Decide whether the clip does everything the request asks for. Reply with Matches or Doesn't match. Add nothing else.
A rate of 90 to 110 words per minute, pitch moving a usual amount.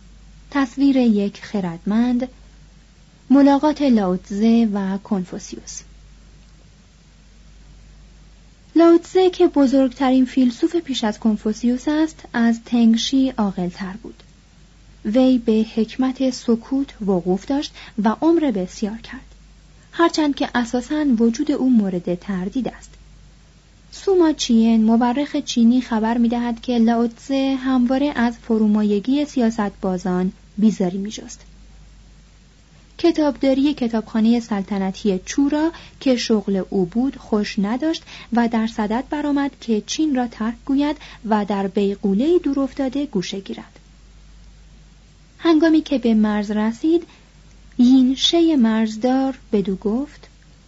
Matches